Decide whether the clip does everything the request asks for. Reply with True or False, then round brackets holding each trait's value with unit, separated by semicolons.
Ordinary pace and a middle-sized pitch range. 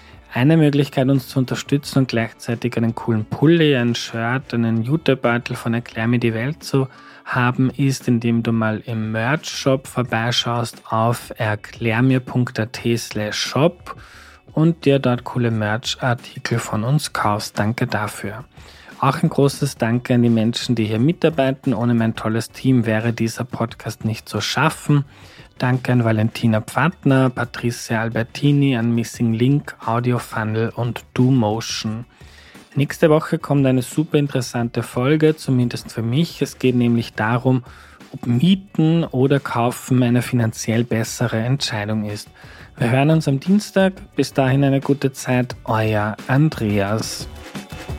True (140 wpm; 3.2 semitones)